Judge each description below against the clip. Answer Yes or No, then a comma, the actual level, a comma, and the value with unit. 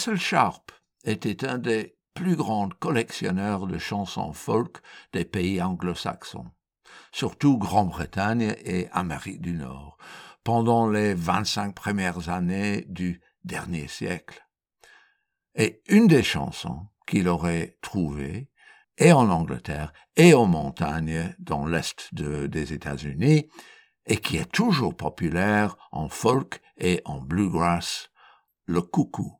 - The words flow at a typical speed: No, slow, 120 wpm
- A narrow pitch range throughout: No, average, 5.0 semitones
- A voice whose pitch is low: Yes, very low, 95 Hz